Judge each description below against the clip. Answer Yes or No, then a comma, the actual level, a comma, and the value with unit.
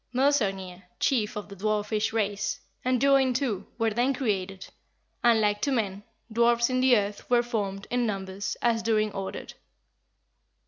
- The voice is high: Yes, high, 220 Hz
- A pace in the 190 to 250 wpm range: No, average, 150 wpm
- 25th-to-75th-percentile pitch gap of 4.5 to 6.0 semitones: No, average, 3.3 semitones